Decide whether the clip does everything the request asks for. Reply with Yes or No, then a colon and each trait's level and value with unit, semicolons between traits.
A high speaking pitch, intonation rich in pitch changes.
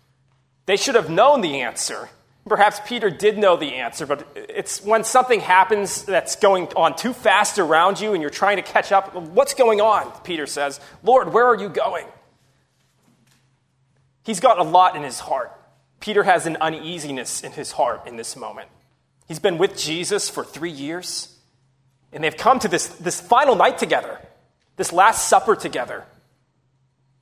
No: medium, 180 Hz; wide, 7.8 semitones